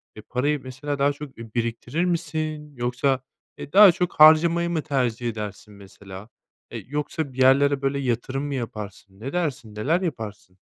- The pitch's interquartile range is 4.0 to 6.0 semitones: Yes, average, 4.6 semitones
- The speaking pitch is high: No, low, 135 Hz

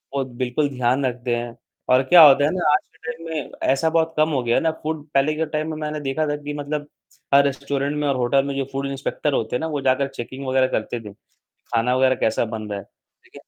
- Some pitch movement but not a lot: Yes, average, 3.0 semitones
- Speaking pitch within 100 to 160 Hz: Yes, medium, 140 Hz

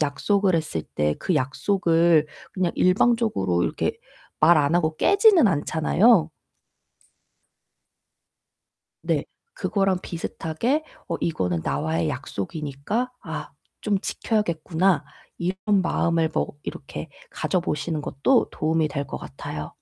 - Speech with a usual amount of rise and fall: Yes, average, 4.8 semitones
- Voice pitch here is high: No, medium, 165 Hz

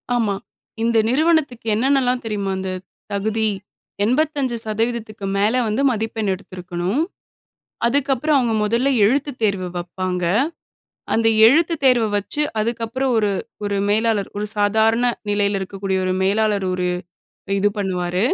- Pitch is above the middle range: Yes, high, 220 Hz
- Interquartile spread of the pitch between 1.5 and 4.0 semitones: Yes, average, 3.7 semitones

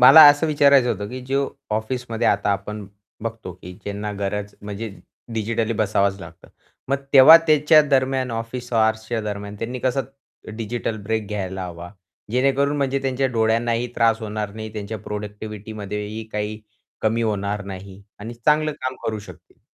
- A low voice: Yes, low, 110 Hz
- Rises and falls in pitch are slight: No, average, 3.6 semitones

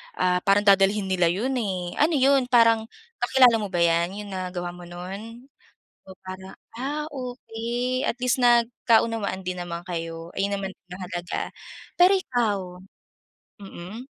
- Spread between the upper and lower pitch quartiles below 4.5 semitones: No, average, 5.1 semitones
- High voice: Yes, high, 200 Hz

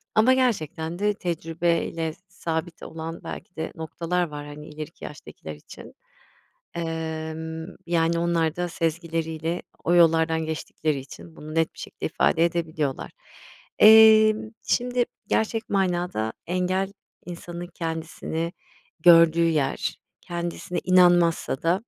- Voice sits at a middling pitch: Yes, medium, 165 Hz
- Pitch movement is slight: Yes, narrow, 1.7 semitones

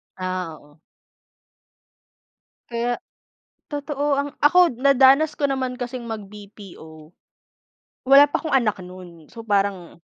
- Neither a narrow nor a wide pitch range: No, wide, 7.0 semitones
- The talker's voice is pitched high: Yes, high, 235 Hz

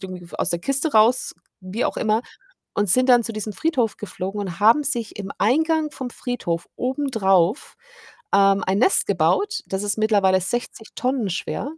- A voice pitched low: No, high, 220 Hz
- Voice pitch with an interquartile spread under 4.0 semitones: No, average, 4.8 semitones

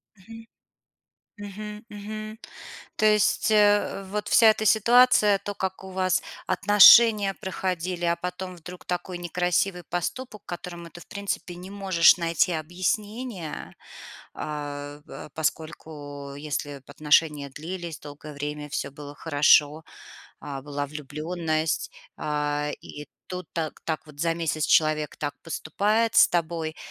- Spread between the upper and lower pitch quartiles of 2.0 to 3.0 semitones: No, average, 4.8 semitones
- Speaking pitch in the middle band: Yes, medium, 175 Hz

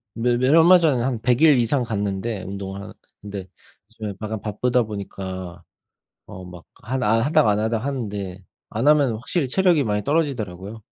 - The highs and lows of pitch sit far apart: No, average, 4.7 semitones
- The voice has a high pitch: No, low, 110 Hz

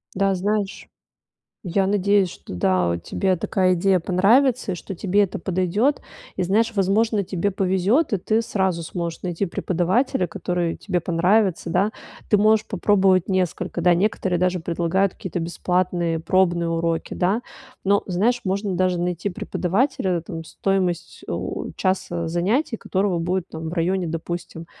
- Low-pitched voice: No, medium, 185 Hz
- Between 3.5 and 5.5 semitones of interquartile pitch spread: No, narrow, 2.6 semitones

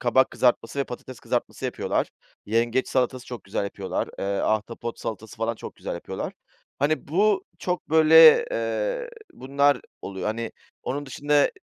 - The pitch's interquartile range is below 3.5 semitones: No, average, 5.1 semitones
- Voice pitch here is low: Yes, low, 130 Hz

